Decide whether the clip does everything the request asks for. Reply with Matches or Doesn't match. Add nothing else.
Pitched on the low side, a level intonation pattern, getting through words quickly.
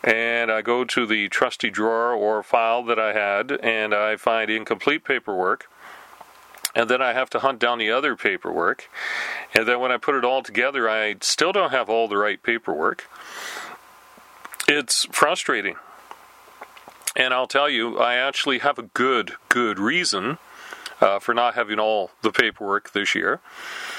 Doesn't match